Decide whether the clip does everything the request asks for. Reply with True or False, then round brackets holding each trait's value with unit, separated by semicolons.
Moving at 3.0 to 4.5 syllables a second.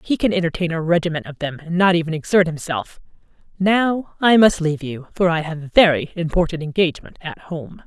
False (5.8 syllables/s)